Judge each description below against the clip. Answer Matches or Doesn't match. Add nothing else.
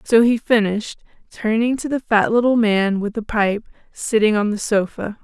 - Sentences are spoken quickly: Doesn't match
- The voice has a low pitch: Doesn't match